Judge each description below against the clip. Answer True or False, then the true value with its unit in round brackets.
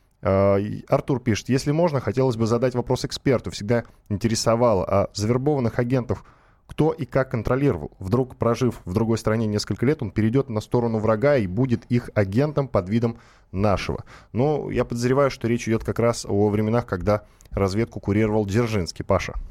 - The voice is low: True (115 Hz)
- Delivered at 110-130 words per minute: False (160 wpm)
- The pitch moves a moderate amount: True (3.5 semitones)